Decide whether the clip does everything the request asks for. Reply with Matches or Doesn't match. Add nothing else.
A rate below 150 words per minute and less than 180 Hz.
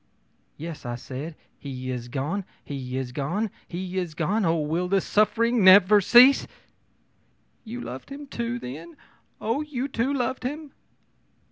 Doesn't match